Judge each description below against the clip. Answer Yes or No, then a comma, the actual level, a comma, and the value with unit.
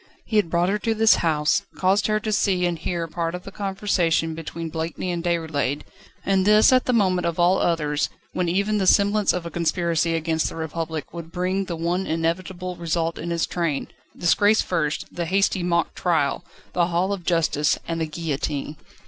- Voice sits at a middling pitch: Yes, medium, 170 Hz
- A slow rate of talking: No, average, 190 wpm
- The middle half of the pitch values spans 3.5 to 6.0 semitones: No, narrow, 2.5 semitones